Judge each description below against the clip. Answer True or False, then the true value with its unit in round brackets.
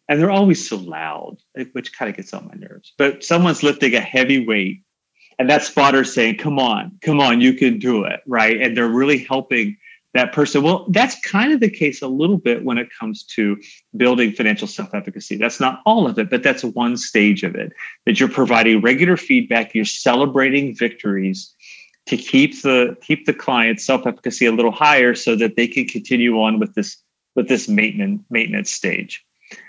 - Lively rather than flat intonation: True (5.7 semitones)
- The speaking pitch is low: True (130 Hz)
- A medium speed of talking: True (190 wpm)